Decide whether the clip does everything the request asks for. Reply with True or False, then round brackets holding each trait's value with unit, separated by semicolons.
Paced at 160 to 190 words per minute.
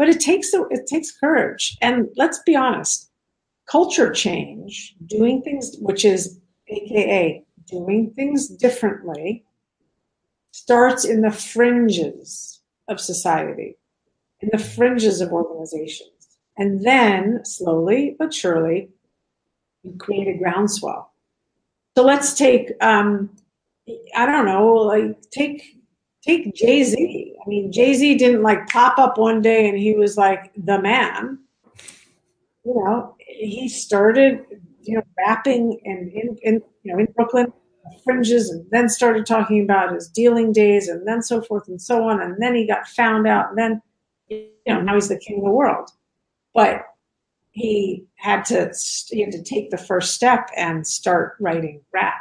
False (150 wpm)